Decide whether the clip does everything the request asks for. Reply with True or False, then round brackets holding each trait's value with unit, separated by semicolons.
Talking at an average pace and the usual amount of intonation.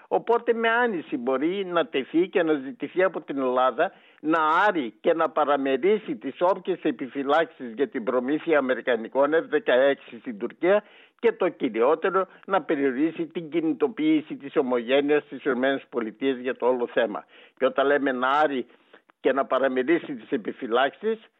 False (145 wpm; 6.9 semitones)